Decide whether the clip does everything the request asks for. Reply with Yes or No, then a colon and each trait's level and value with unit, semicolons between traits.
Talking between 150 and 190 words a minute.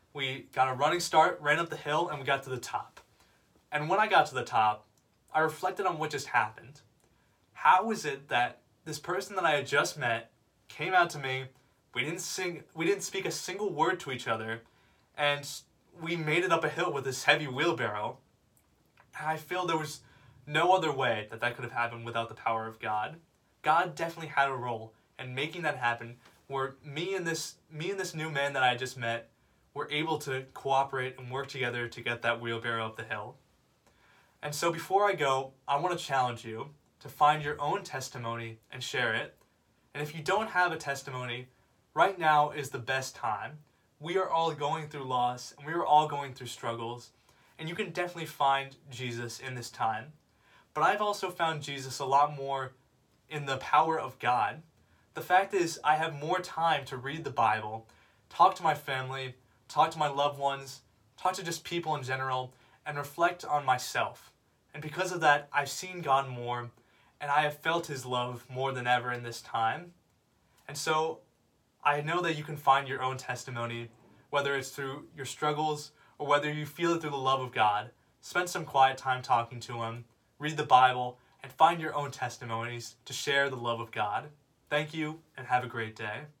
No: average, 200 wpm